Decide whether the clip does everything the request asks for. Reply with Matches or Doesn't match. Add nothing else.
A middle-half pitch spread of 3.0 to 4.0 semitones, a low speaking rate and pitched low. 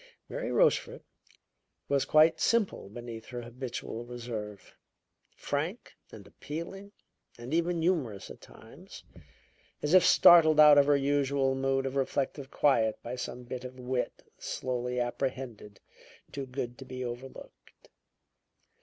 Matches